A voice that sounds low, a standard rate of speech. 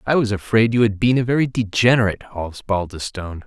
Yes: low, 105 Hz; average, 175 wpm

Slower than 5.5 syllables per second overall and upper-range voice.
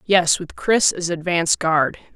No: 4.2 syllables/s; medium, 170 Hz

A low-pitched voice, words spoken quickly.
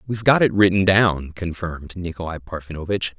No: very low, 90 Hz; average, 150 wpm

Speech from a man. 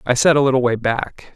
Yes: male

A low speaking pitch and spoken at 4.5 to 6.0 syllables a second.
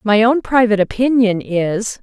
No: high, 220 Hz; 4.7 syllables/s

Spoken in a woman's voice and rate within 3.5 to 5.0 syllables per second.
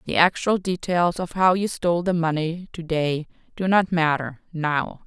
Yes: female; 4.5 syllables/s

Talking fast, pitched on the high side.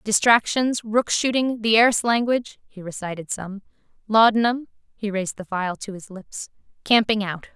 No: average, 145 wpm; high, 215 Hz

